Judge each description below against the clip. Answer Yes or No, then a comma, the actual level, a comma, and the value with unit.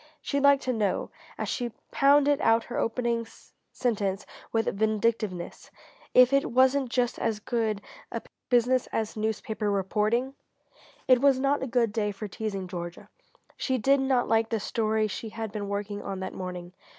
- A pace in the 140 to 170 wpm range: Yes, average, 160 wpm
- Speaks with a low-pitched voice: No, high, 225 Hz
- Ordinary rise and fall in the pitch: Yes, average, 3.5 semitones